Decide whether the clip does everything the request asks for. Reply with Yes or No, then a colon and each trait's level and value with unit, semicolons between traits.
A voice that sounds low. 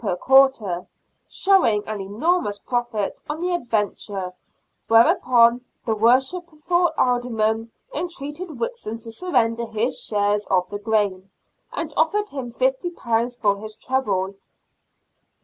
No: high, 235 Hz